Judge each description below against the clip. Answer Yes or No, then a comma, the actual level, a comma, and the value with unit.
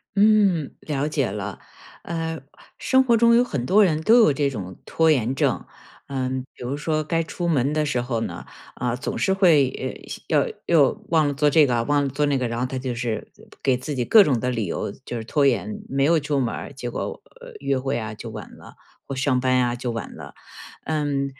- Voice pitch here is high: No, medium, 140 Hz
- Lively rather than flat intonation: No, average, 4.2 semitones